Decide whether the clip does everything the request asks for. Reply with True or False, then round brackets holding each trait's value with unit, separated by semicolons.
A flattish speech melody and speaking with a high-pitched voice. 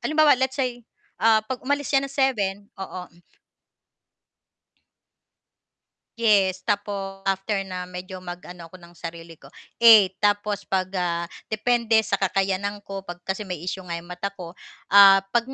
False (3.3 semitones; 195 Hz)